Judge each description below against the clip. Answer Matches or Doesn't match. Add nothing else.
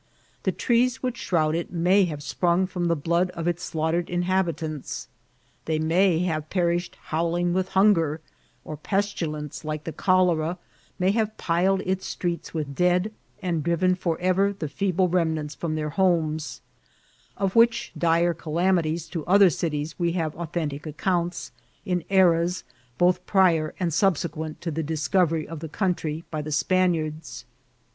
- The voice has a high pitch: Doesn't match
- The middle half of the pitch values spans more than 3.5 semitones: Doesn't match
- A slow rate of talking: Doesn't match